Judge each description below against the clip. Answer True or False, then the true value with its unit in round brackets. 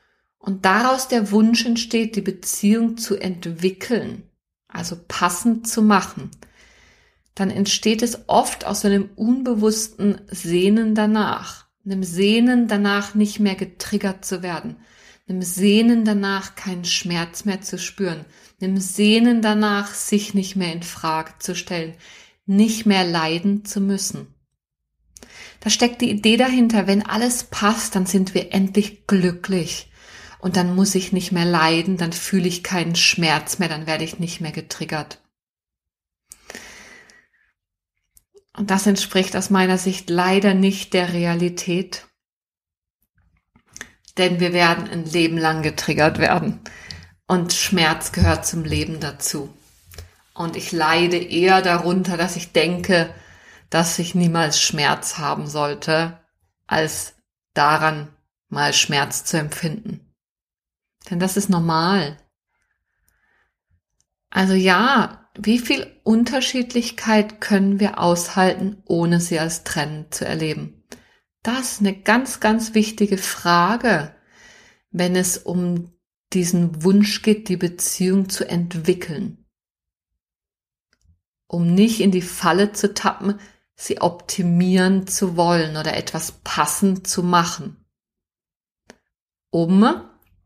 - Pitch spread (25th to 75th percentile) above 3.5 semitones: False (3.2 semitones)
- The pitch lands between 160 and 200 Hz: True (185 Hz)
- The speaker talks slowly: True (120 wpm)